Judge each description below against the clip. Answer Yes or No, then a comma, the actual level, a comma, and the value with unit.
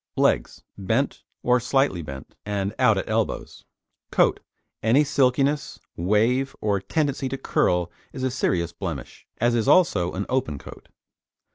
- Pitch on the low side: Yes, low, 110 Hz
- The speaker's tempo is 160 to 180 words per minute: No, average, 140 wpm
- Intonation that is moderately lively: No, wide, 6.1 semitones